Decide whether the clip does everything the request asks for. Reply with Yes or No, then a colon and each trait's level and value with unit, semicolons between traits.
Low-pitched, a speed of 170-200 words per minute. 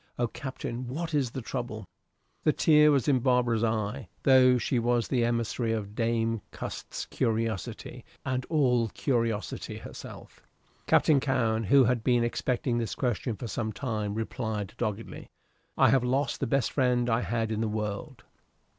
No: low, 120 Hz; average, 155 wpm